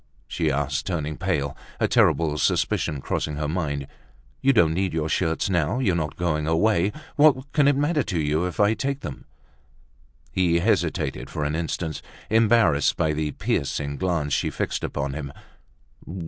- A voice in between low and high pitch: No, very low, 80 Hz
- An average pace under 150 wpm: No, average, 160 wpm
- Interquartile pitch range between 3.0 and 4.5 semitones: No, wide, 5.4 semitones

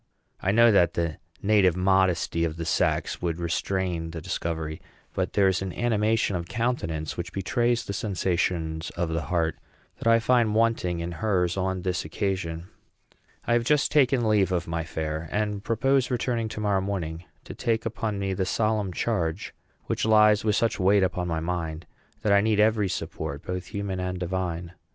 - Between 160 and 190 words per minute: Yes, average, 180 wpm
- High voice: No, very low, 95 Hz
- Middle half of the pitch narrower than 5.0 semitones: Yes, average, 4.2 semitones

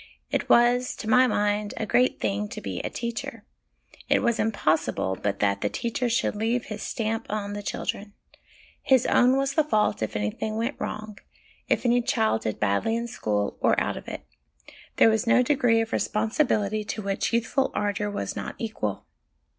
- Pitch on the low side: No, high, 220 Hz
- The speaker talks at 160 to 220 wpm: Yes, average, 180 wpm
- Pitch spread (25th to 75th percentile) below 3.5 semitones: Yes, average, 2.8 semitones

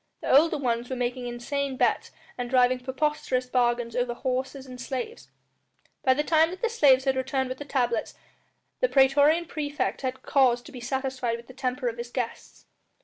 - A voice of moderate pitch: No, very high, 260 Hz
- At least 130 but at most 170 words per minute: No, average, 185 wpm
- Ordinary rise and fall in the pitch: No, narrow, 2.3 semitones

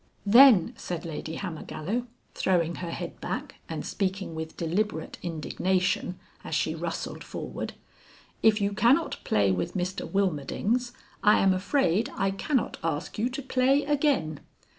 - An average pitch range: No, wide, 6.2 semitones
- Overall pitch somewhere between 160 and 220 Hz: Yes, high, 190 Hz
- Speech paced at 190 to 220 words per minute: No, average, 140 wpm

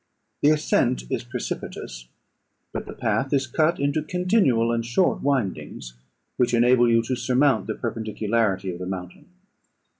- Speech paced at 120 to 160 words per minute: Yes, average, 145 wpm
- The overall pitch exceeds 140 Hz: No, low, 120 Hz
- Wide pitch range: No, average, 4.8 semitones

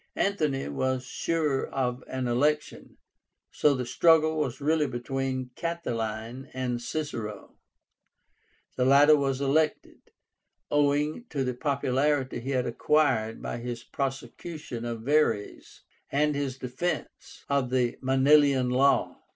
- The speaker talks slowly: Yes, slow, 120 wpm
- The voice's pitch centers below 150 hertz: Yes, low, 135 Hz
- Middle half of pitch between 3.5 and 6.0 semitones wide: No, average, 3.1 semitones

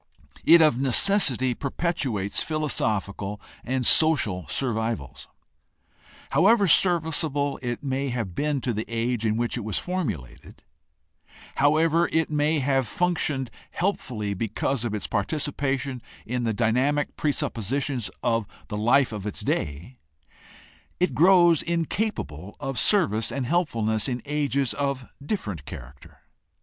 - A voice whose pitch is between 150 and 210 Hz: No, low, 130 Hz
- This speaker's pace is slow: Yes, slow, 125 wpm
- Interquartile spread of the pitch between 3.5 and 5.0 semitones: No, wide, 5.6 semitones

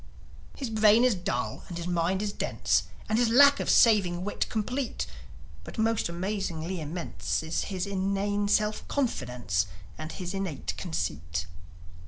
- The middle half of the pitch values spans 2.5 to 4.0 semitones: No, average, 4.8 semitones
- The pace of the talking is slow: No, average, 145 wpm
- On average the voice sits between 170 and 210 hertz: Yes, high, 190 Hz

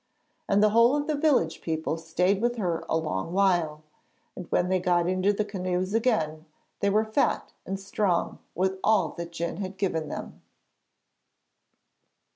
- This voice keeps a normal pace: Yes, average, 160 wpm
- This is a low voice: No, medium, 185 Hz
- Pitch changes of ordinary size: Yes, average, 3.6 semitones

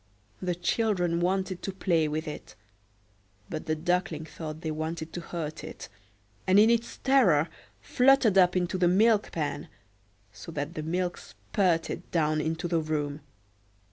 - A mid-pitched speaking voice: Yes, medium, 170 Hz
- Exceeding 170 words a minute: No, average, 150 wpm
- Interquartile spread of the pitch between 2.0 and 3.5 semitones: Yes, average, 3.0 semitones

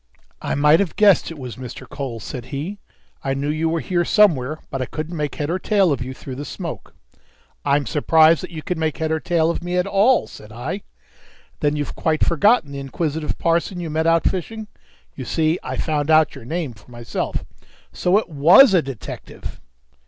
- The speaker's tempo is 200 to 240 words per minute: Yes, fast, 205 wpm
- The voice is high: No, medium, 155 Hz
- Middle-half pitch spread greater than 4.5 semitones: No, average, 3.9 semitones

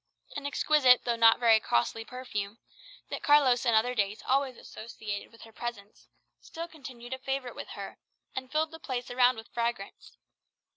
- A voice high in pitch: Yes, high, 245 Hz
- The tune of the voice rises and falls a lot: No, average, 2.9 semitones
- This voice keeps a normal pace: Yes, average, 165 wpm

